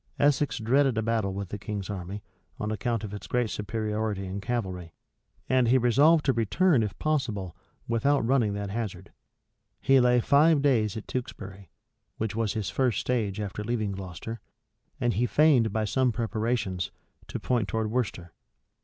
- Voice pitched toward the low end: Yes, low, 110 Hz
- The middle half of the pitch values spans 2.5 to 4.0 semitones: Yes, average, 3.5 semitones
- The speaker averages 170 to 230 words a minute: No, average, 160 wpm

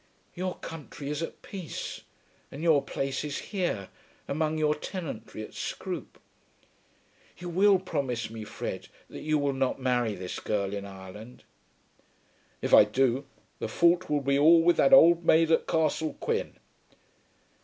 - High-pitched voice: No, medium, 145 Hz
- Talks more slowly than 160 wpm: Yes, average, 150 wpm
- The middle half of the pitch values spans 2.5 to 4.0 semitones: No, average, 5.2 semitones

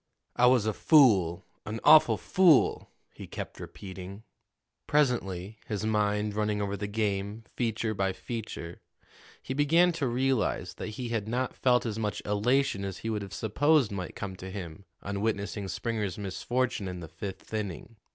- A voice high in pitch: No, low, 105 Hz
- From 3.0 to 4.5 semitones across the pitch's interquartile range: Yes, average, 3.8 semitones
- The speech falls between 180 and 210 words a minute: No, average, 160 wpm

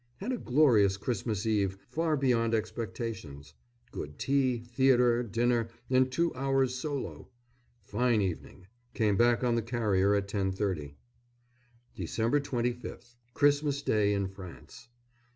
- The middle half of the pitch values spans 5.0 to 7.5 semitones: No, average, 4.1 semitones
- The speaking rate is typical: No, slow, 120 wpm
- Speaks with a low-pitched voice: Yes, low, 115 Hz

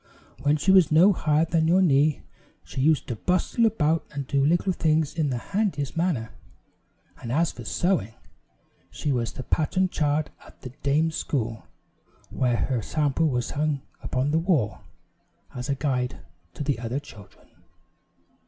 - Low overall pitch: No, medium, 150 Hz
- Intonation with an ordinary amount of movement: Yes, average, 4.2 semitones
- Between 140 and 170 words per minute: Yes, average, 160 wpm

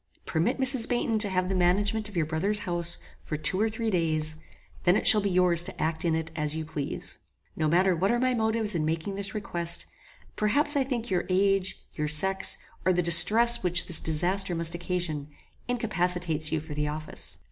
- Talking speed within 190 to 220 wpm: Yes, average, 200 wpm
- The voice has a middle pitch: Yes, medium, 180 Hz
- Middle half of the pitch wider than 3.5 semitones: Yes, average, 4.5 semitones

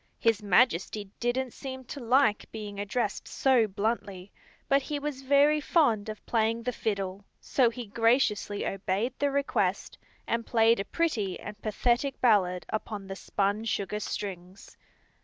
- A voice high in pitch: Yes, high, 225 Hz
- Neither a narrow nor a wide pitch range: Yes, average, 4.1 semitones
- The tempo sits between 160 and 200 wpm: No, average, 145 wpm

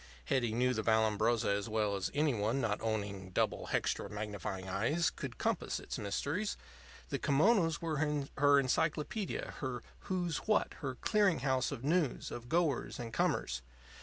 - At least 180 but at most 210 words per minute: No, average, 150 wpm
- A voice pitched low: Yes, low, 125 Hz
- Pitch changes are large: Yes, wide, 6.4 semitones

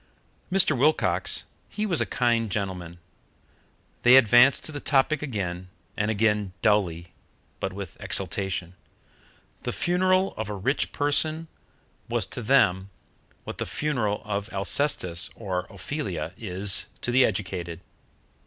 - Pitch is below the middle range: Yes, low, 105 Hz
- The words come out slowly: Yes, slow, 125 wpm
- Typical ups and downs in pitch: No, wide, 6.8 semitones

